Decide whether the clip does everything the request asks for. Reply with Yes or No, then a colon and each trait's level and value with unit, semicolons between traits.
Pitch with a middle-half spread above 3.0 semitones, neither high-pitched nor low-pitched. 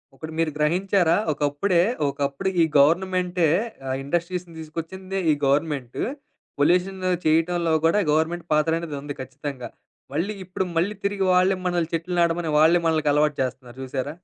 Yes: average, 3.6 semitones; medium, 165 Hz